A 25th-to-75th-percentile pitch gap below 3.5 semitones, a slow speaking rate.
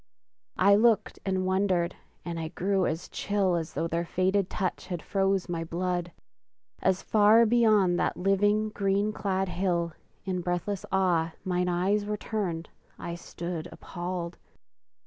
No: narrow, 2.5 semitones; average, 145 wpm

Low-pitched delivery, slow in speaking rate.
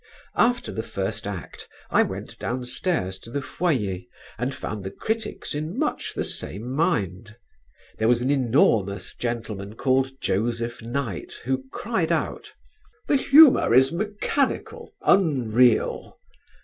Yes: low, 125 Hz; slow, 125 wpm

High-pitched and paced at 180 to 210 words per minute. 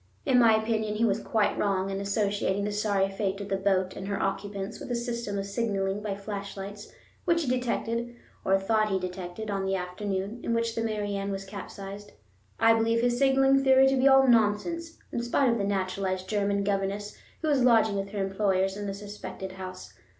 Yes: high, 205 Hz; fast, 205 wpm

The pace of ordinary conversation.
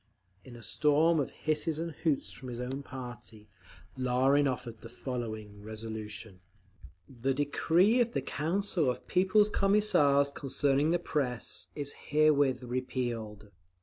No: slow, 130 wpm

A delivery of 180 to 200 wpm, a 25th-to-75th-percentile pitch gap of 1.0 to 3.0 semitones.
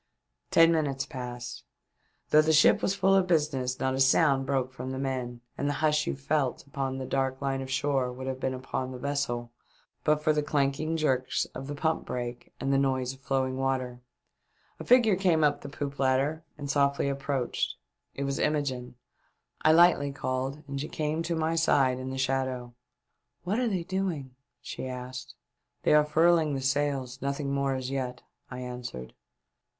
Yes: average, 190 wpm; narrow, 2.6 semitones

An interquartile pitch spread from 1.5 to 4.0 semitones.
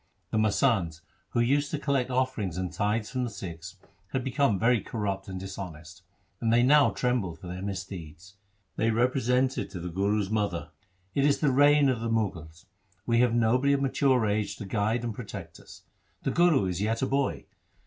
No: average, 5.0 semitones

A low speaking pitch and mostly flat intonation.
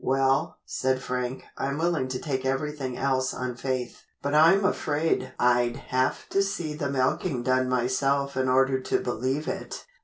Yes: low, 130 Hz; narrow, 2.2 semitones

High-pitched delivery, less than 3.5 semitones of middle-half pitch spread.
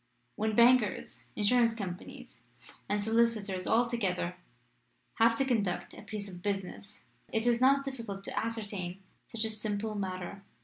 Yes: high, 215 Hz; average, 2.9 semitones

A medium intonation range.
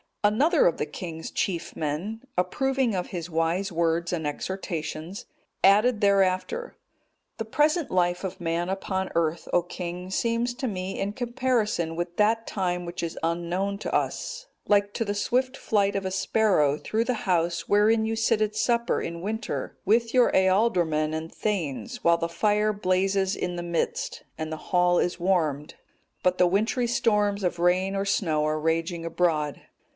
Yes: average, 4.1 semitones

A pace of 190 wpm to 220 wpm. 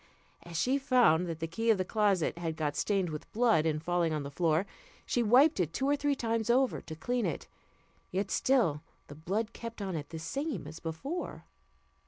Yes: fast, 205 wpm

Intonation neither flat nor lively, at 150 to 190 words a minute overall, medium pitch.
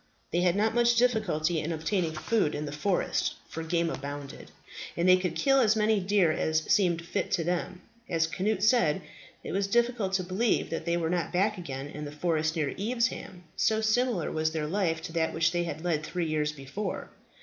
No: average, 4.5 semitones; fast, 205 wpm; medium, 175 Hz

